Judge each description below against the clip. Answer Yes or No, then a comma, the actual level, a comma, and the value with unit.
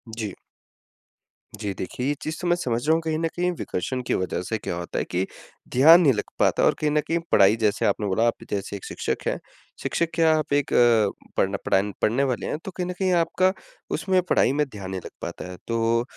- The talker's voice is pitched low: Yes, low, 125 Hz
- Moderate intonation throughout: No, wide, 7.8 semitones